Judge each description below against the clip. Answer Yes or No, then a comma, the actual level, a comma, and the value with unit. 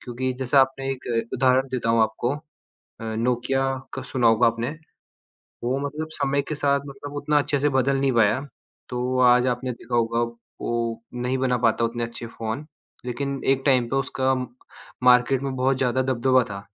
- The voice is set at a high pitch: No, low, 130 Hz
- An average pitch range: No, narrow, 2.3 semitones